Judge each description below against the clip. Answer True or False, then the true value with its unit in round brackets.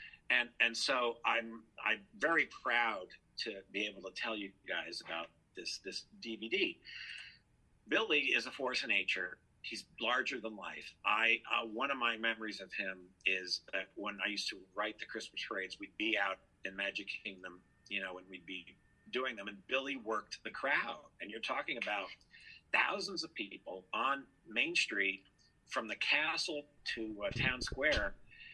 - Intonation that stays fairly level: False (3.5 semitones)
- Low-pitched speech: True (100 Hz)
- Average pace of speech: True (170 wpm)